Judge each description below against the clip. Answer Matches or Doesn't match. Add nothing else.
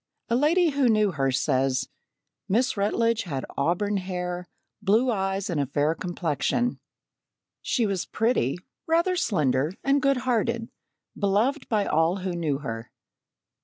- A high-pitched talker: Matches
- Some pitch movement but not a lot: Doesn't match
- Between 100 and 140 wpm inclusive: Matches